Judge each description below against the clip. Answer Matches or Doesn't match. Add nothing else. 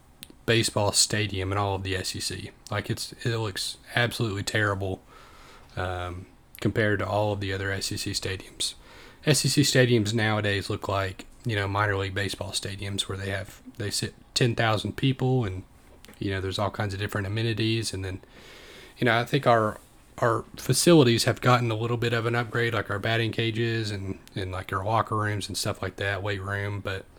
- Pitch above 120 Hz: Doesn't match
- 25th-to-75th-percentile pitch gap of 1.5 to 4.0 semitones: Matches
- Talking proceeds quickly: Doesn't match